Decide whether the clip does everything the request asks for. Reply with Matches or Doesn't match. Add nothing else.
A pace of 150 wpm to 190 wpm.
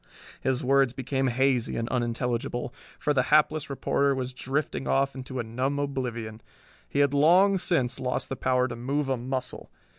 Matches